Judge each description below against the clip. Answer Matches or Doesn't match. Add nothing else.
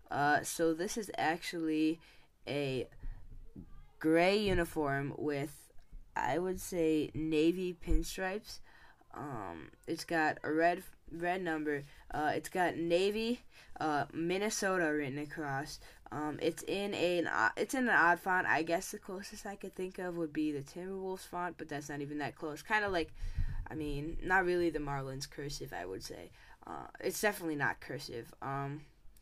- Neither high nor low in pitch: Matches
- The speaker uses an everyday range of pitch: Matches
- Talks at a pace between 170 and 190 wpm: Doesn't match